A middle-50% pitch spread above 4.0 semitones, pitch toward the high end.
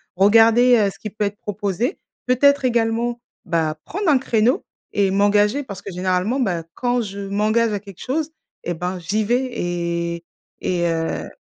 Yes: average, 4.7 semitones; high, 205 Hz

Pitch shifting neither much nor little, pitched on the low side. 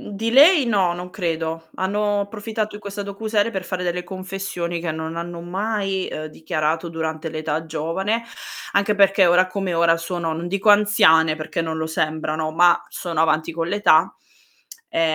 No: average, 3.7 semitones; medium, 175 Hz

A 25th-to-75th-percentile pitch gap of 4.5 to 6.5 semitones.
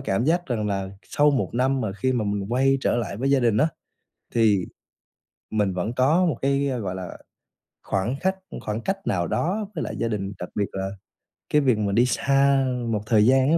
Yes: average, 5.1 semitones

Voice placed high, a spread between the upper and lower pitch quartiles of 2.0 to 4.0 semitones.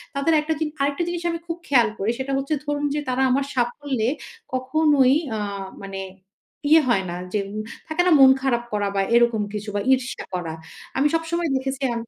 No: very high, 265 Hz; average, 4.5 semitones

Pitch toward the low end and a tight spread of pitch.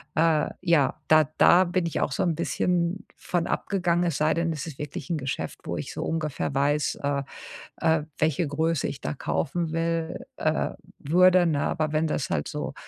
No: medium, 160 Hz; narrow, 2.3 semitones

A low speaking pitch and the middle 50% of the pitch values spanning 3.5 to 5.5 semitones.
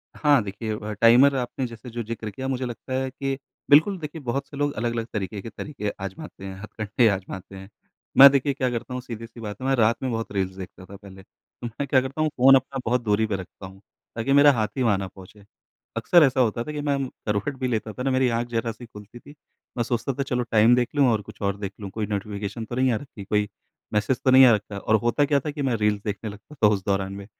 Yes: low, 115 Hz; average, 4.2 semitones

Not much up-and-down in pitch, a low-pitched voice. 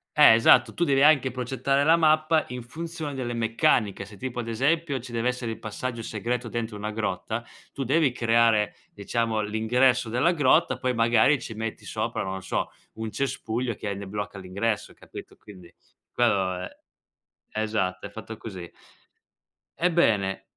No: average, 3.8 semitones; low, 115 Hz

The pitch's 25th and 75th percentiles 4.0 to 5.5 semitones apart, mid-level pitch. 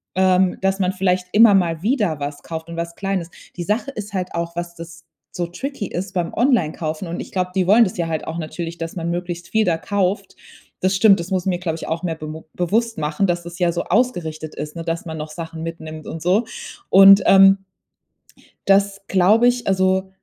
No: average, 2.8 semitones; medium, 180 Hz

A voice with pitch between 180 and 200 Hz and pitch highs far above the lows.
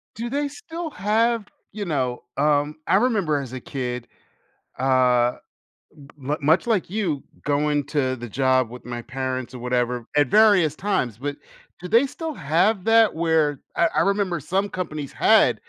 No: medium, 150 Hz; wide, 7.8 semitones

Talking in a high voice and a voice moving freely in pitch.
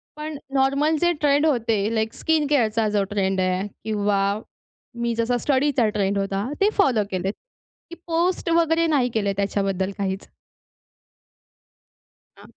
Yes: high, 230 Hz; wide, 6.8 semitones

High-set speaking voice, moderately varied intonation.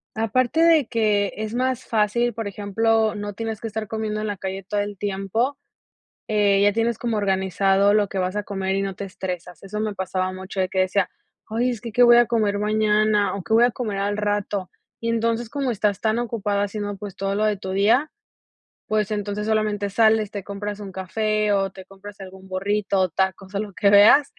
No: high, 205 Hz; narrow, 2.1 semitones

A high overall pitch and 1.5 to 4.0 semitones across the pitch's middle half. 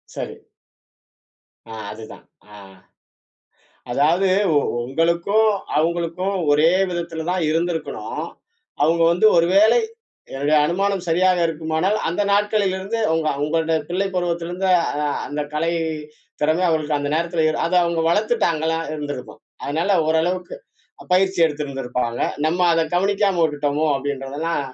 No: medium, 165 Hz; average, 3.2 semitones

